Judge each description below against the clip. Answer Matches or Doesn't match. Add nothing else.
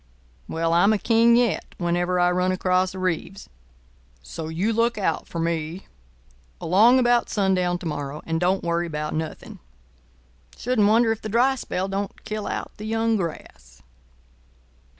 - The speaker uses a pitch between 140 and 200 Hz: Matches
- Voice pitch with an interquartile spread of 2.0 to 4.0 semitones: Doesn't match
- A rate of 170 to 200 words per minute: Doesn't match